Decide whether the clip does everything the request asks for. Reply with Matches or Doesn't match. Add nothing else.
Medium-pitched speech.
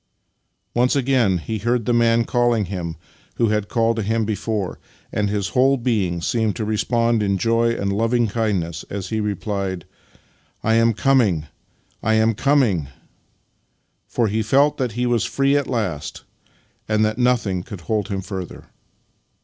Doesn't match